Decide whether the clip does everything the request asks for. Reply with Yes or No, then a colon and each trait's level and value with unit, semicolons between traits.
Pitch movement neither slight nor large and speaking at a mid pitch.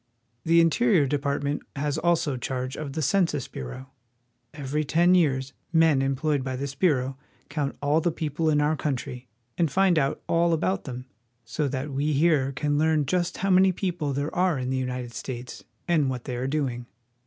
Yes: average, 3.6 semitones; medium, 145 Hz